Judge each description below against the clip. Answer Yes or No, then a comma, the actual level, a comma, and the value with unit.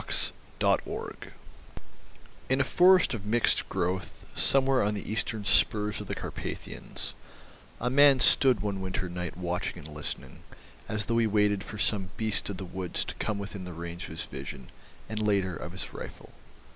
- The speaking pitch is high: No, low, 100 Hz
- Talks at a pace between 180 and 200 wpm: No, average, 170 wpm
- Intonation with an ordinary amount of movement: Yes, average, 3.6 semitones